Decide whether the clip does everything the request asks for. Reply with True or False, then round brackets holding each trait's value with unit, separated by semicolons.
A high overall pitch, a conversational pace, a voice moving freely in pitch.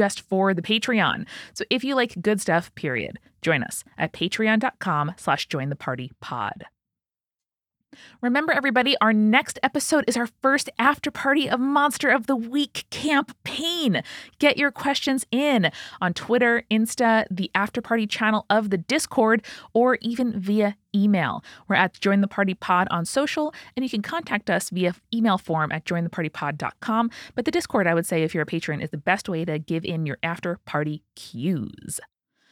True (215 Hz; 170 wpm; 6.7 semitones)